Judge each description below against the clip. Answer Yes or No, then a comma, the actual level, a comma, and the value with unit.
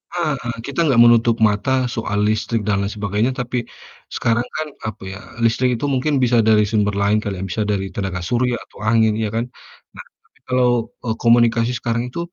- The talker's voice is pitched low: Yes, low, 115 Hz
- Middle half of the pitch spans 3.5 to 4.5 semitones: No, average, 2.7 semitones